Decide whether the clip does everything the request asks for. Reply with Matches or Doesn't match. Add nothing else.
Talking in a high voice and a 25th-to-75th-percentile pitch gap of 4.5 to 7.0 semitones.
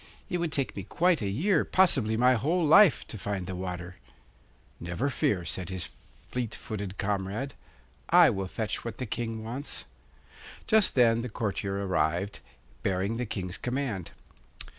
Doesn't match